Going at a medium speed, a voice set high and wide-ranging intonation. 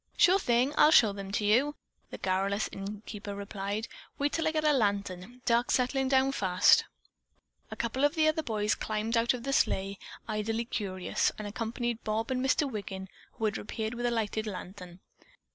No: average, 180 wpm; high, 220 Hz; average, 4.0 semitones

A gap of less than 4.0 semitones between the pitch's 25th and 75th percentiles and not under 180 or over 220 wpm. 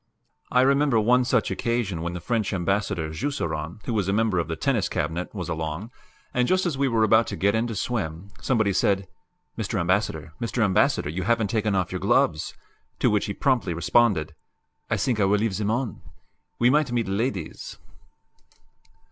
No: average, 4.8 semitones; average, 185 wpm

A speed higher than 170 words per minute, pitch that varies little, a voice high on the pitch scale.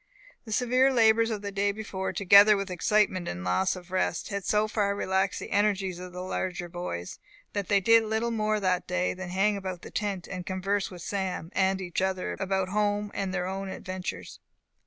Yes: average, 200 wpm; narrow, 2.1 semitones; high, 195 Hz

